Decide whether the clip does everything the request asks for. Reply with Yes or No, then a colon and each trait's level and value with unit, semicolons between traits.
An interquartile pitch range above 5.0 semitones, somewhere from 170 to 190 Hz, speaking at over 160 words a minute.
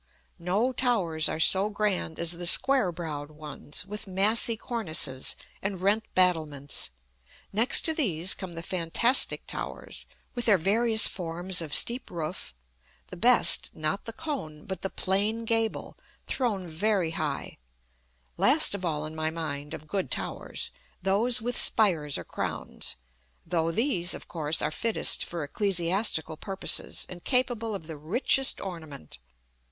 No: wide, 5.6 semitones; medium, 185 Hz; average, 145 wpm